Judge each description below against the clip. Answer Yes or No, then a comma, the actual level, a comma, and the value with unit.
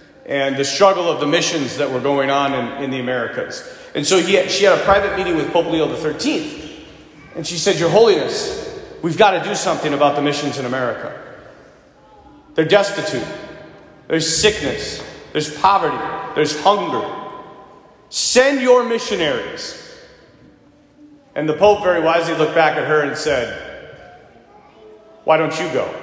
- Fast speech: No, average, 155 wpm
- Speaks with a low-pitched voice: No, medium, 185 Hz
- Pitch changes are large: Yes, wide, 7.4 semitones